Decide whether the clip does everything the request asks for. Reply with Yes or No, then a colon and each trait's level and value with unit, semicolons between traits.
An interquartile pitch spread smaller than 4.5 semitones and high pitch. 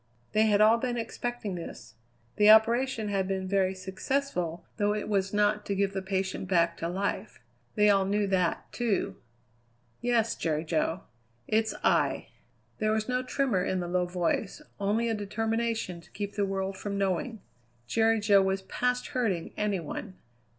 Yes: average, 2.8 semitones; high, 205 Hz